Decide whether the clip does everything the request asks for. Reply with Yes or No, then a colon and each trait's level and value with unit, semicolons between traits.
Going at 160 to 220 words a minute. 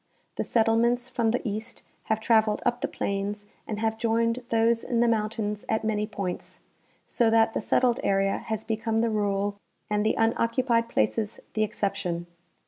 Yes: average, 170 wpm